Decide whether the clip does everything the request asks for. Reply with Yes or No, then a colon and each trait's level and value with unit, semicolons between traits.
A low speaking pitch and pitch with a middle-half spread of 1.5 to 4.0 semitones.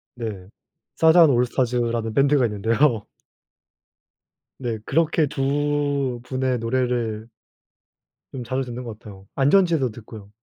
Yes: low, 125 Hz; average, 3.7 semitones